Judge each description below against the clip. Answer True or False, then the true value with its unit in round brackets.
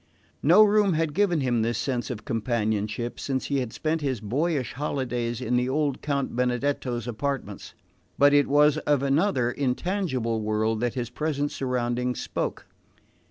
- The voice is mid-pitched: False (130 Hz)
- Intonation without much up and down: False (3.5 semitones)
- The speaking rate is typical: True (155 wpm)